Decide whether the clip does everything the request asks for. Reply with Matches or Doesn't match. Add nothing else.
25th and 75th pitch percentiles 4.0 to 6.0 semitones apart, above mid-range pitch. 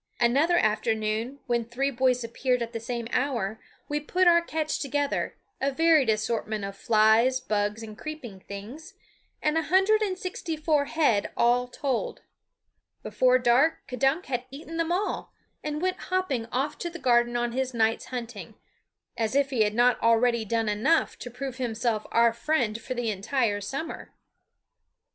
Matches